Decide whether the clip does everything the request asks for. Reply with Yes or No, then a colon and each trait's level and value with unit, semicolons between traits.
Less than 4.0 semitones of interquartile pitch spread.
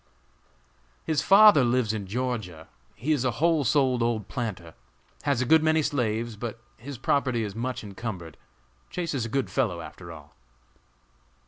No: average, 4.5 semitones